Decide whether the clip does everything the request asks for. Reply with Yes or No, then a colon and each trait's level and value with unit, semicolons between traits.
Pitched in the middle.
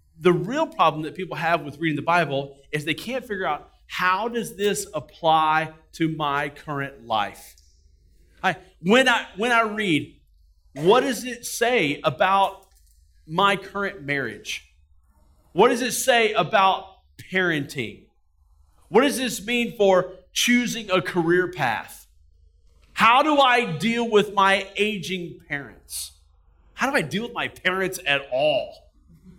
Yes: medium, 175 Hz